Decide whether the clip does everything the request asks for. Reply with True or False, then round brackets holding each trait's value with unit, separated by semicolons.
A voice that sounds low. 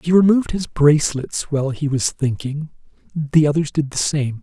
False (150 Hz)